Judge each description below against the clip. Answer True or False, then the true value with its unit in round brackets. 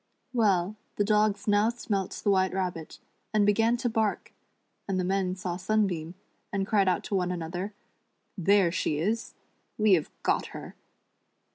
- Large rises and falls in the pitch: False (2.8 semitones)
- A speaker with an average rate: True (165 wpm)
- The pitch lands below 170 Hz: False (195 Hz)